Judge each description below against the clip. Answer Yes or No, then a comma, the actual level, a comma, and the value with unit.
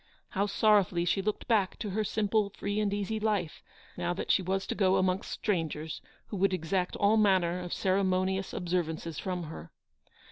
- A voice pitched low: No, high, 190 Hz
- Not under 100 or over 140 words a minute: No, average, 180 wpm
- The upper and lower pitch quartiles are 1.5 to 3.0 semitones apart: Yes, narrow, 2.5 semitones